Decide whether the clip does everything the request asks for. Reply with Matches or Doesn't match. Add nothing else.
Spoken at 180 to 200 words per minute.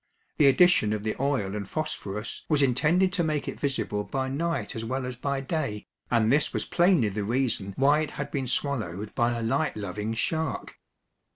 Matches